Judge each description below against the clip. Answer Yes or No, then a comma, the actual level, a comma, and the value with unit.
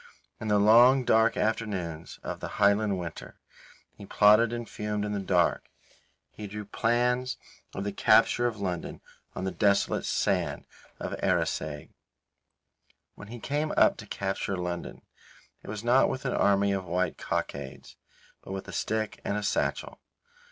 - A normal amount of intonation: Yes, average, 3.0 semitones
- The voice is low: Yes, low, 105 Hz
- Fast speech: No, average, 155 wpm